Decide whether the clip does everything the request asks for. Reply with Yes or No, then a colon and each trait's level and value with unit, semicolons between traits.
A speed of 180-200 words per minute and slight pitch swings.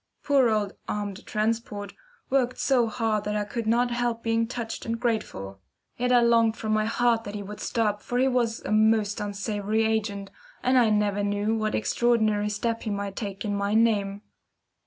Yes: average, 185 wpm; narrow, 2.1 semitones